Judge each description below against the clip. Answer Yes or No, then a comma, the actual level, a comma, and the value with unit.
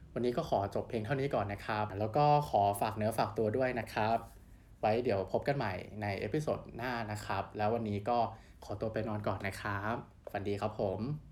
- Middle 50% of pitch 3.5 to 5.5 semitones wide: No, narrow, 2.4 semitones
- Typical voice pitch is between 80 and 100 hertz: No, low, 110 Hz